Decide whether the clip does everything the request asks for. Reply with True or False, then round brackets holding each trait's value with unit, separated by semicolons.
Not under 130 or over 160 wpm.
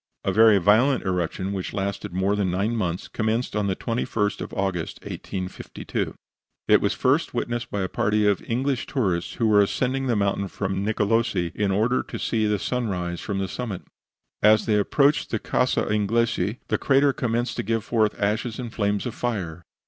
False (180 wpm)